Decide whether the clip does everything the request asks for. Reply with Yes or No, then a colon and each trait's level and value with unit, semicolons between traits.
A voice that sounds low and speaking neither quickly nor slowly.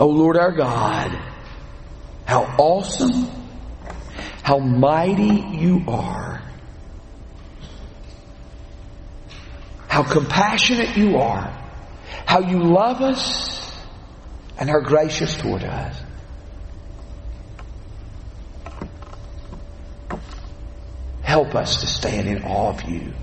No: low, 100 Hz; slow, 80 wpm